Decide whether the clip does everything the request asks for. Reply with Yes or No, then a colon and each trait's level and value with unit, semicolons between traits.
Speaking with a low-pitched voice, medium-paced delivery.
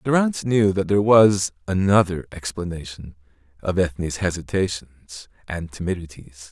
No: very low, 90 Hz; slow, 110 wpm